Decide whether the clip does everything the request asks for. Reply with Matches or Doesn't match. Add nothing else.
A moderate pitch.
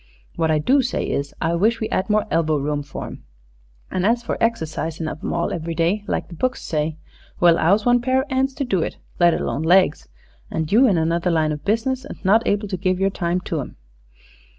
Matches